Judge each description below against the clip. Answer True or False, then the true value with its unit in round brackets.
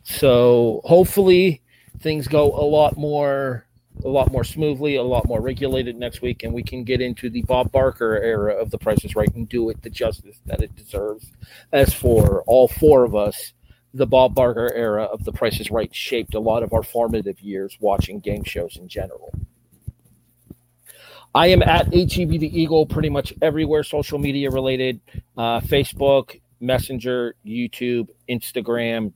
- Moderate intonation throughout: True (3.3 semitones)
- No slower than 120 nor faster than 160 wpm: False (175 wpm)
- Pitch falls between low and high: False (125 Hz)